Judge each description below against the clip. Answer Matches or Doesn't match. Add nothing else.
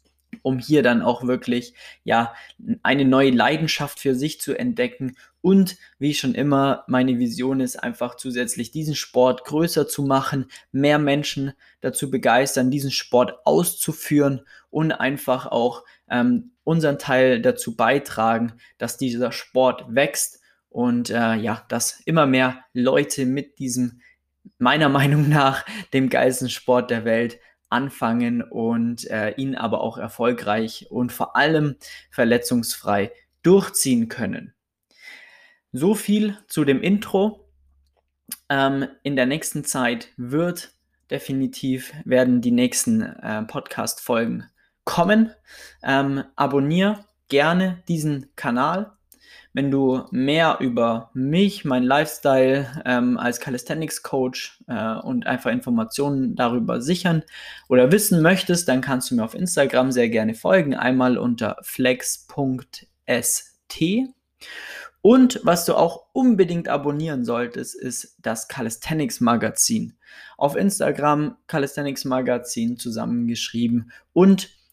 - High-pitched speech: Doesn't match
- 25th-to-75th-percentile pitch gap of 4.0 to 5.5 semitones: Matches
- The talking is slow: Matches